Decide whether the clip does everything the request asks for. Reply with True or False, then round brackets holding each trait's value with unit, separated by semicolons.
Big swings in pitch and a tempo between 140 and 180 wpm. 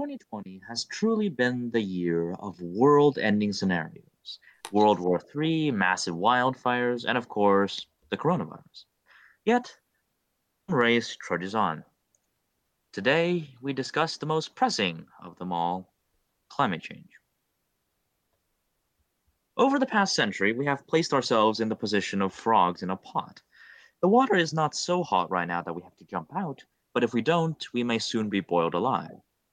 True (8.5 semitones; 150 wpm)